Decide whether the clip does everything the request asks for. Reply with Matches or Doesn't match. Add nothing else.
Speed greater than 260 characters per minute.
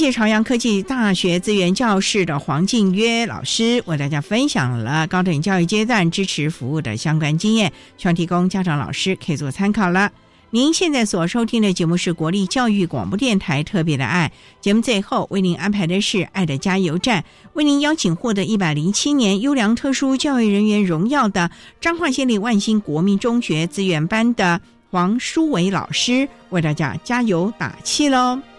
Matches